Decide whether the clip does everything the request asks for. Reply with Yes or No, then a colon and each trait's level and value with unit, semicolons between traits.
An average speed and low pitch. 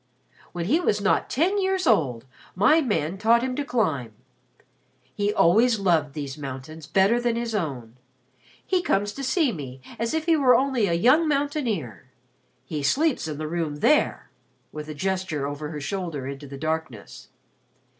No: average, 165 wpm; high, 190 Hz